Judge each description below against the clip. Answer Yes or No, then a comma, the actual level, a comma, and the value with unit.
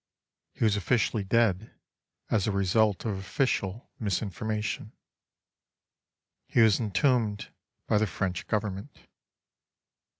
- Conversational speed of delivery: No, slow, 100 wpm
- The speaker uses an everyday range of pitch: No, narrow, 2.3 semitones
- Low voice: Yes, low, 105 Hz